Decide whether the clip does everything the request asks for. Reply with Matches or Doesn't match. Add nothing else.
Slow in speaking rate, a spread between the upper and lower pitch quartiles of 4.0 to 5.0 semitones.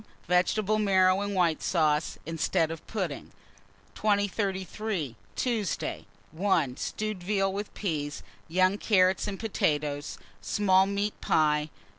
Matches